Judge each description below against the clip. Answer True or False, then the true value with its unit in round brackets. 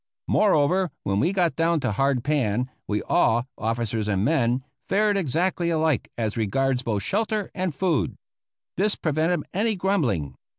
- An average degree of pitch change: False (7.9 semitones)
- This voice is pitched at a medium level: True (145 Hz)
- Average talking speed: True (145 wpm)